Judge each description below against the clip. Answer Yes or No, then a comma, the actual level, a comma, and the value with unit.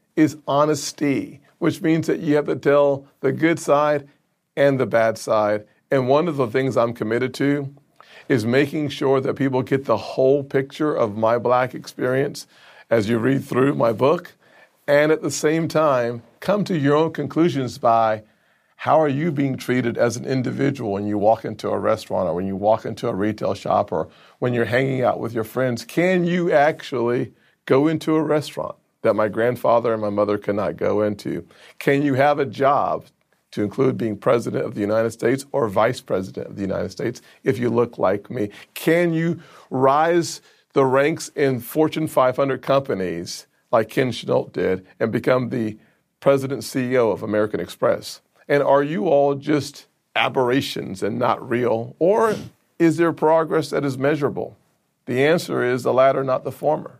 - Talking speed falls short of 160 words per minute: No, average, 180 wpm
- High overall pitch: No, low, 135 Hz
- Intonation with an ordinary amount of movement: Yes, average, 4.1 semitones